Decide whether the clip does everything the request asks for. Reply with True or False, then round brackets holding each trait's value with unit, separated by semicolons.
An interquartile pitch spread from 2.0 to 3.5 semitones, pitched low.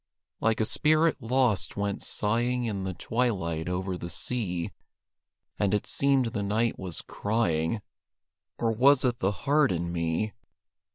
False (4.9 semitones; 105 Hz)